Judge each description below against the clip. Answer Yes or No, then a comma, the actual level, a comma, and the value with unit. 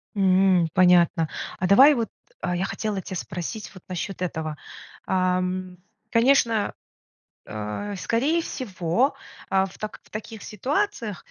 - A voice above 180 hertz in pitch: Yes, high, 190 Hz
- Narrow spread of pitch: No, average, 3.7 semitones